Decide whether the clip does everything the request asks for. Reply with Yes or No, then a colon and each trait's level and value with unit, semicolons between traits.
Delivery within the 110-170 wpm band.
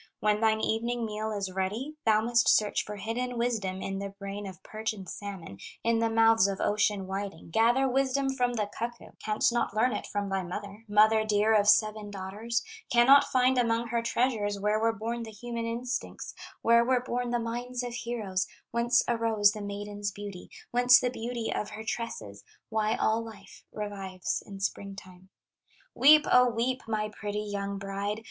No: average, 180 wpm